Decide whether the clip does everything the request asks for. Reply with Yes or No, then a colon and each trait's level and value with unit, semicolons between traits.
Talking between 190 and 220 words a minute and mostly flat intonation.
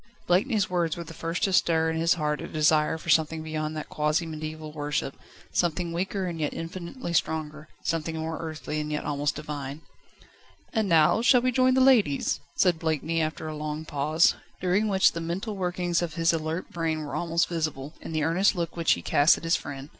Yes: average, 200 wpm; narrow, 2.3 semitones